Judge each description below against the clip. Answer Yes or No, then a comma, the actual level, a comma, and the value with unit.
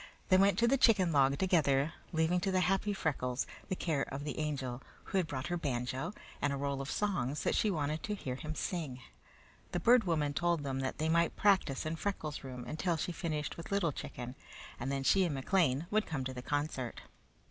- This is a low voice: No, medium, 155 Hz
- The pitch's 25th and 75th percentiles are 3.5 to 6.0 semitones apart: Yes, average, 5.0 semitones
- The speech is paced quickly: Yes, fast, 210 wpm